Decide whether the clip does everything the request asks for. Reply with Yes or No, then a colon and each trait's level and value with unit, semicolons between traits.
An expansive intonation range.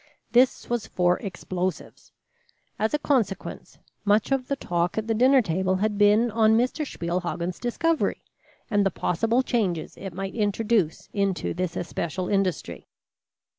No: average, 4.3 semitones